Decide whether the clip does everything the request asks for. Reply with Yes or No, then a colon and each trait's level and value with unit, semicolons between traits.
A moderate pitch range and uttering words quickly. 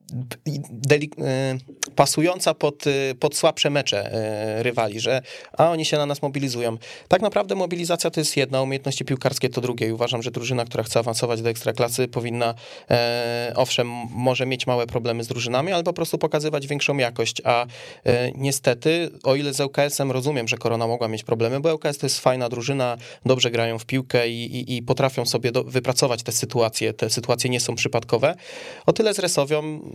Yes: average, 3.3 semitones; fast, 185 wpm